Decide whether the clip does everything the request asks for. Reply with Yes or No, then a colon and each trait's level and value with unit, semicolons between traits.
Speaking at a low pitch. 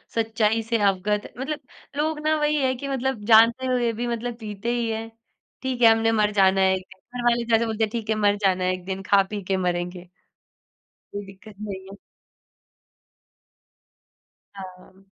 No: high, 220 Hz